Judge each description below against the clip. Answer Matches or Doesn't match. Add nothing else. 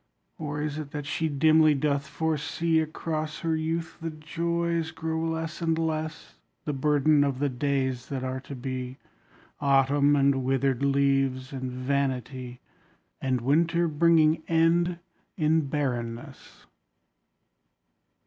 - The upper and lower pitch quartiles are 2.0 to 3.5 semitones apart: Matches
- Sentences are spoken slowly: Matches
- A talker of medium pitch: Matches